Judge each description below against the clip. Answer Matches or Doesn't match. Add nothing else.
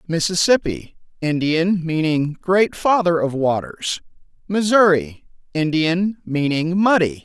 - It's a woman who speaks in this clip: Doesn't match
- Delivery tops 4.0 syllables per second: Doesn't match